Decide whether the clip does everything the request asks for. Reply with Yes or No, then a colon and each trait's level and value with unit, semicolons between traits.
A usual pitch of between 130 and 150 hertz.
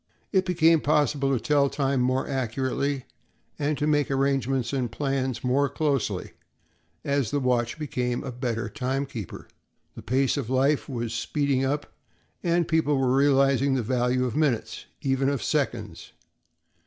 Yes: low, 135 Hz